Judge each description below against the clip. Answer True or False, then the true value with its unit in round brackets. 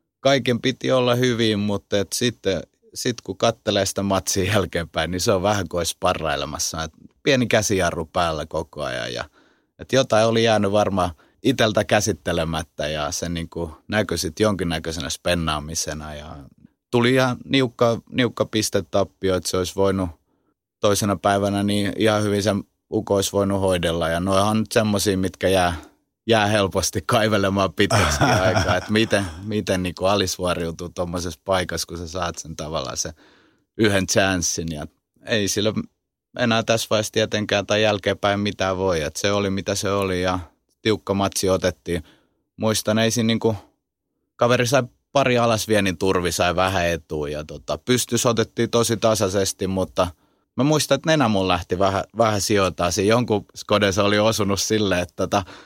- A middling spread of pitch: True (3.3 semitones)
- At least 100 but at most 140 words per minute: False (150 wpm)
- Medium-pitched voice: False (100 Hz)